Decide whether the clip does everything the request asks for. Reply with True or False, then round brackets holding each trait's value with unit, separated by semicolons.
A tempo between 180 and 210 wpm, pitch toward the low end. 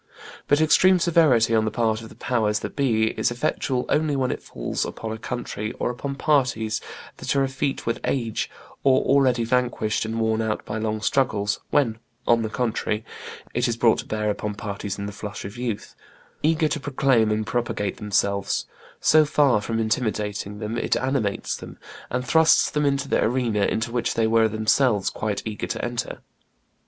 True (185 wpm; 115 Hz)